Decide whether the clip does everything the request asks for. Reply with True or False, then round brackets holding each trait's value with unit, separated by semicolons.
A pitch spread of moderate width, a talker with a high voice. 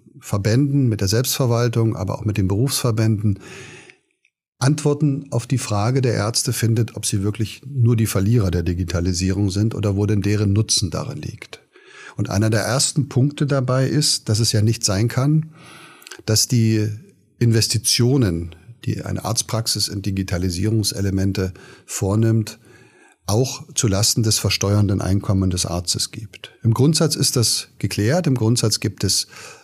False (3.7 semitones; 110 Hz)